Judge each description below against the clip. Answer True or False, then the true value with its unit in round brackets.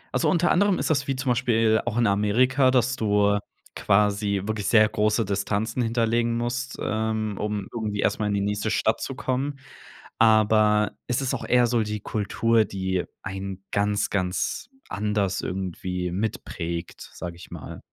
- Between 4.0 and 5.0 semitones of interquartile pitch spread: False (2.8 semitones)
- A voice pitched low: True (110 Hz)